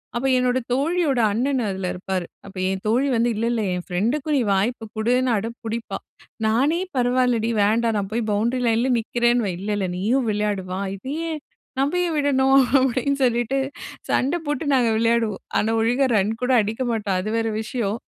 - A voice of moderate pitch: No, high, 235 Hz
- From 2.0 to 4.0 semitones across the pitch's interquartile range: Yes, average, 3.5 semitones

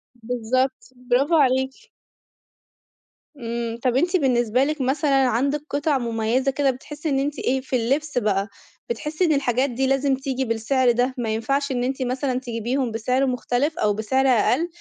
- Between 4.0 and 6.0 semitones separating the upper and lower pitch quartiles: No, narrow, 2.4 semitones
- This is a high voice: Yes, very high, 260 Hz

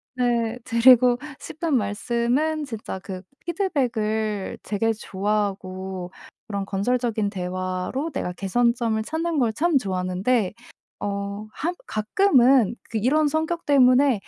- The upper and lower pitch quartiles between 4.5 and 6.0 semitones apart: Yes, average, 5.1 semitones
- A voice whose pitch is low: No, high, 230 Hz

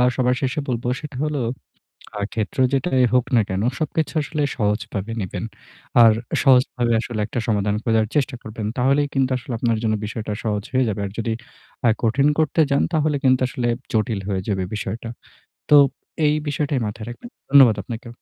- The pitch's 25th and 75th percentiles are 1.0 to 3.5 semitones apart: No, average, 3.9 semitones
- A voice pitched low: Yes, low, 120 Hz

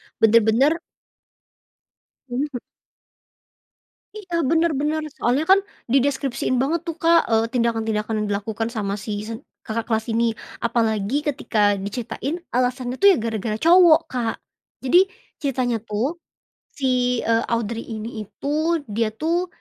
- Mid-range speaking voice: No, high, 245 Hz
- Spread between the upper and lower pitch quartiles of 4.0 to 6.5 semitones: Yes, average, 4.8 semitones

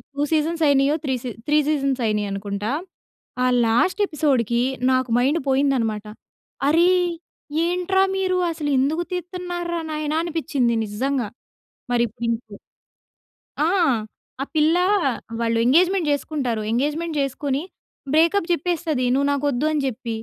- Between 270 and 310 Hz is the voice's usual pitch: Yes, very high, 285 Hz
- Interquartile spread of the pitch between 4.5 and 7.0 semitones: Yes, average, 5.2 semitones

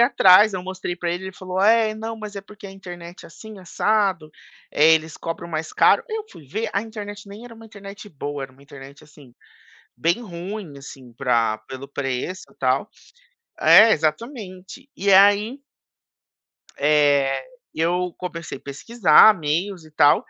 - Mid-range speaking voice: Yes, medium, 180 Hz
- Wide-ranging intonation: Yes, wide, 5.7 semitones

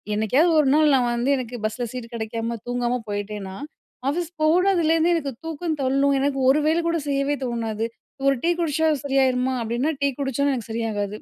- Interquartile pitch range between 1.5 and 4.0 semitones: No, average, 4.9 semitones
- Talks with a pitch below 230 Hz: No, very high, 270 Hz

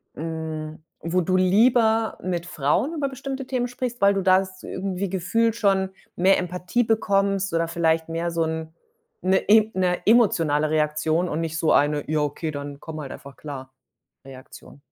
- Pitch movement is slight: No, average, 4.2 semitones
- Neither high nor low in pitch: Yes, medium, 180 Hz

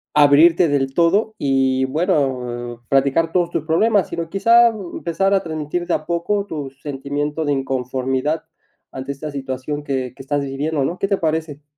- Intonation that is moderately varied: Yes, average, 4.0 semitones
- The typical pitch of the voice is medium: Yes, medium, 150 Hz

